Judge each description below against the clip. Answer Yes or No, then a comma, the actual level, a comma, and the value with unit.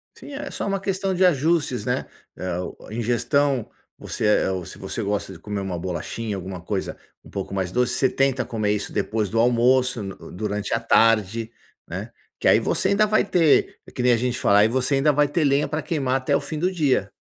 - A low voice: Yes, low, 120 Hz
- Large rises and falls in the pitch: Yes, wide, 5.9 semitones